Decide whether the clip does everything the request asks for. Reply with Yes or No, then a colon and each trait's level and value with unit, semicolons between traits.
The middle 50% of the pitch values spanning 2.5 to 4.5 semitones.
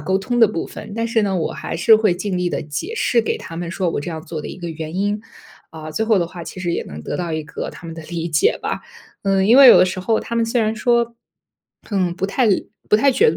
No: average, 5.0 semitones